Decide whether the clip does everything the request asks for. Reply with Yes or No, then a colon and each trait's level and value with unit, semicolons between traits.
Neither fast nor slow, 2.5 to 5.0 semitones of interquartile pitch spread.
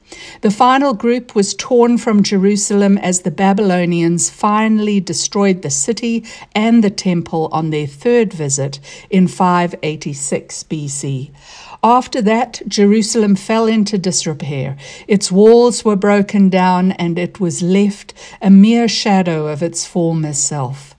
No: slow, 130 wpm; average, 4.3 semitones